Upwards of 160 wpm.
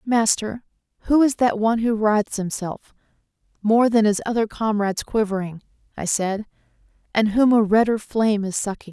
No: average, 155 wpm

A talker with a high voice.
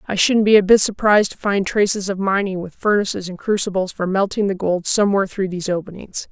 Yes: high, 195 Hz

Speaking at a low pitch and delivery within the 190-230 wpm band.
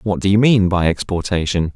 Yes: very low, 95 Hz; fast, 205 wpm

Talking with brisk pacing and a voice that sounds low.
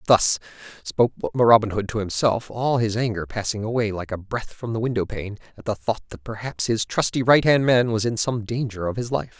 Yes: fast, 210 wpm; low, 110 Hz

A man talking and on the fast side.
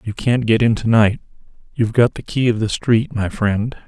Yes: male; fast, 230 wpm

